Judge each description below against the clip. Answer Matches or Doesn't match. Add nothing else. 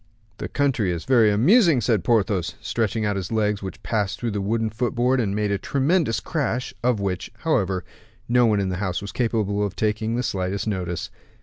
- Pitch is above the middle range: Doesn't match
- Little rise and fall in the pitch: Doesn't match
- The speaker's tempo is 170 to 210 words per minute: Matches